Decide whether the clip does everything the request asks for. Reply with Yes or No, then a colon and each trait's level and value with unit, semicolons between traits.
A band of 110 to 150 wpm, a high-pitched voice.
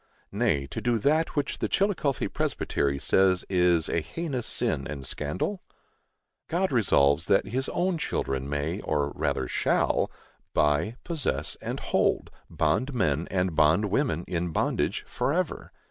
No: average, 140 wpm; very low, 90 Hz